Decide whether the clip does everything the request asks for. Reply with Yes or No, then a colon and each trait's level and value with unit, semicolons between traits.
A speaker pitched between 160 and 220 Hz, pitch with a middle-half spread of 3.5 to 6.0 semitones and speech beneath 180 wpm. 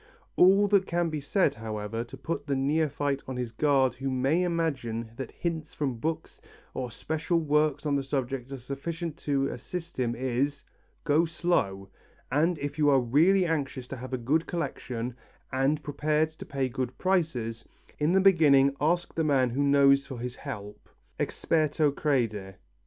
No: medium, 140 Hz; average, 3.9 semitones; average, 170 wpm